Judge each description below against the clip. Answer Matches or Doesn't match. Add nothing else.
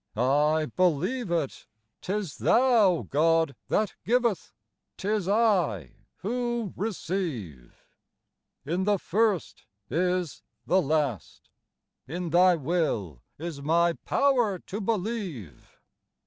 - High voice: Doesn't match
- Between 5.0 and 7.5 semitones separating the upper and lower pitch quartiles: Matches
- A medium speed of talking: Doesn't match